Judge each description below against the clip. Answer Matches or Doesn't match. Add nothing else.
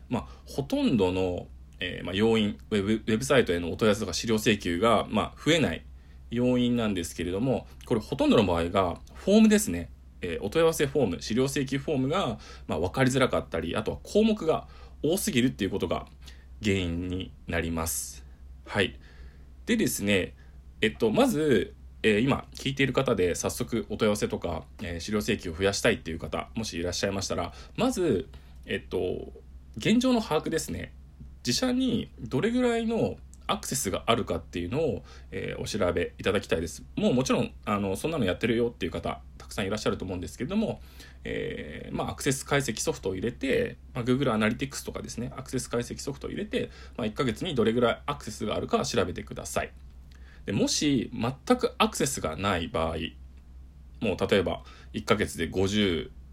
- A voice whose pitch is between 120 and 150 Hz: Doesn't match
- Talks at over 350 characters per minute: Matches